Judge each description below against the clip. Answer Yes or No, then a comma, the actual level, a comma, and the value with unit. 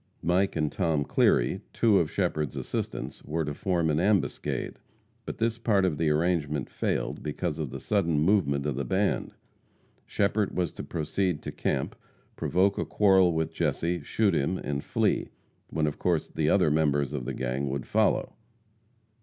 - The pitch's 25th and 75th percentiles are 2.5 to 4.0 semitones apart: No, average, 4.4 semitones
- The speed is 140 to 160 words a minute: No, average, 170 wpm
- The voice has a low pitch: Yes, very low, 80 Hz